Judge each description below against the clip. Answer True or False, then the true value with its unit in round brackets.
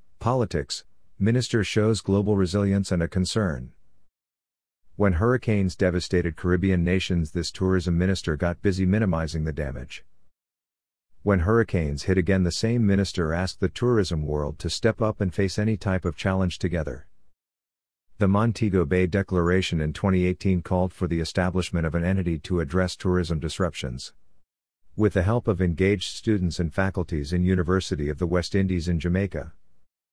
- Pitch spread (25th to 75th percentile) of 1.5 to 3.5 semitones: True (2.5 semitones)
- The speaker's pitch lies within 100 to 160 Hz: False (90 Hz)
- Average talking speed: True (150 wpm)